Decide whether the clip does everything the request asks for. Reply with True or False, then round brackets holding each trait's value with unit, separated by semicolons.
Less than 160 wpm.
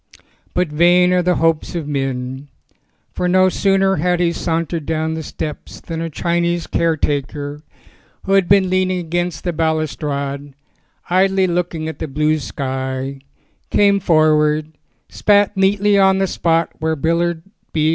True (145 wpm)